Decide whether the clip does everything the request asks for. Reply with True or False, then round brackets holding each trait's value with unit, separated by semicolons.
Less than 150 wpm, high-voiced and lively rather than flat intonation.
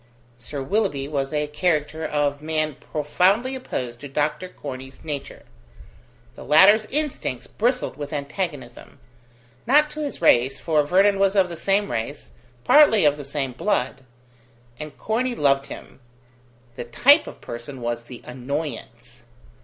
False (140 wpm; 150 Hz; 6.2 semitones)